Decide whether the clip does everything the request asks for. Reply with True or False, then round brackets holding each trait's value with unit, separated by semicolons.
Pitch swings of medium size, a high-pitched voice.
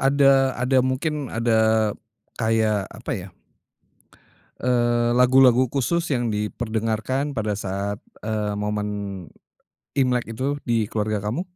False (3.3 semitones; 115 Hz)